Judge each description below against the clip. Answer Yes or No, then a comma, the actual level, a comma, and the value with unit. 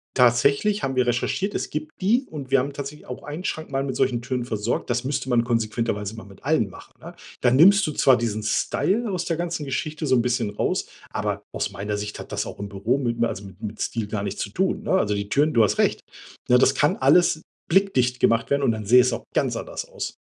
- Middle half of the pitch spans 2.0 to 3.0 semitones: No, average, 5.3 semitones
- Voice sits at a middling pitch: No, low, 125 Hz